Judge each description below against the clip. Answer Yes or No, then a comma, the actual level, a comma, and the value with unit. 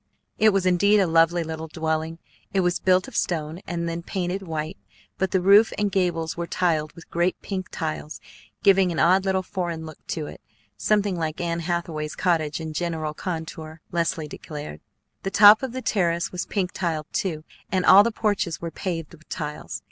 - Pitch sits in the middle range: Yes, medium, 170 Hz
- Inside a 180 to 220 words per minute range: Yes, average, 185 wpm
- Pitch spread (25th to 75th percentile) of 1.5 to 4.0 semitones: Yes, average, 2.8 semitones